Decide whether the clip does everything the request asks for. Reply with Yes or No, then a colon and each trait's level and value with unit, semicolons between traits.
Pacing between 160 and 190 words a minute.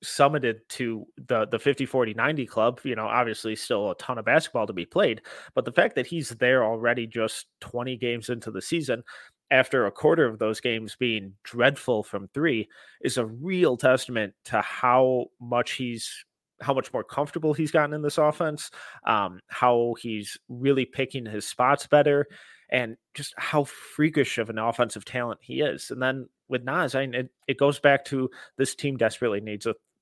Yes: average, 185 wpm